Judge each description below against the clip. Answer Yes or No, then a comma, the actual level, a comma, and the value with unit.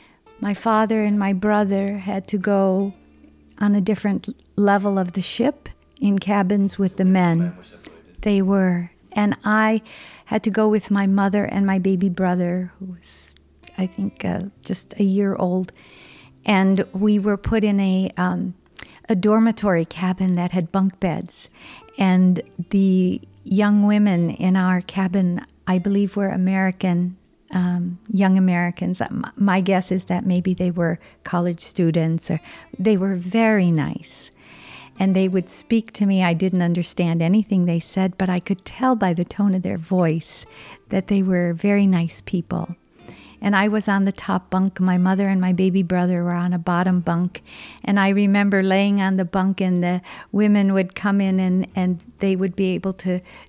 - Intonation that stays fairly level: Yes, narrow, 1.9 semitones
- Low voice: No, high, 190 Hz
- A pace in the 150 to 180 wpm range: Yes, average, 170 wpm